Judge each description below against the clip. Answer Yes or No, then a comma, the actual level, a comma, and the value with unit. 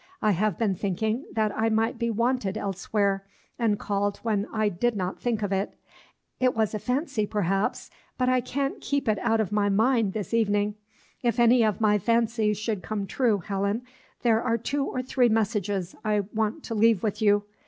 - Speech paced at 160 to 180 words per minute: No, average, 190 wpm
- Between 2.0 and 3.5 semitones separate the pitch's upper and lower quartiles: Yes, narrow, 2.4 semitones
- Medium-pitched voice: No, high, 215 Hz